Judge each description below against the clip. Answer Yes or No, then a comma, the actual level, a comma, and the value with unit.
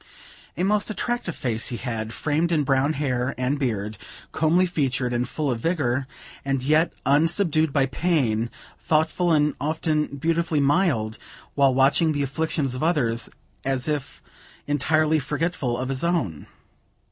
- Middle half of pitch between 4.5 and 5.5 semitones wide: No, average, 3.9 semitones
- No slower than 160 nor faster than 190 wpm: No, average, 145 wpm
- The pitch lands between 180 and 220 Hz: No, medium, 145 Hz